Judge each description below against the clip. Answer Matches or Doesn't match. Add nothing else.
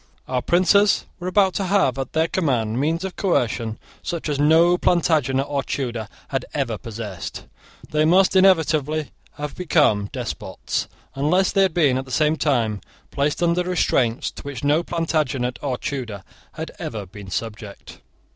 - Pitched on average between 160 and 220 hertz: Doesn't match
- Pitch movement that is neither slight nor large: Doesn't match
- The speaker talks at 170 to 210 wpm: Doesn't match